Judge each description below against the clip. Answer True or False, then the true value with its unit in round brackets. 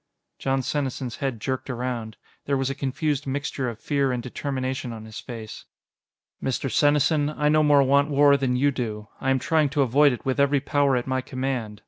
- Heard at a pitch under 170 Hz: True (135 Hz)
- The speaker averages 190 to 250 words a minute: True (195 wpm)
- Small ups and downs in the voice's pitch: True (2.3 semitones)